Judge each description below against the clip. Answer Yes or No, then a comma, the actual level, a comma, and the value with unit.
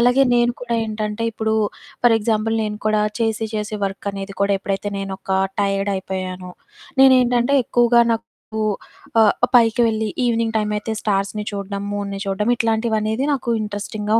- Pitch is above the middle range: Yes, high, 215 Hz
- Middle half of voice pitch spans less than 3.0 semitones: Yes, narrow, 2.5 semitones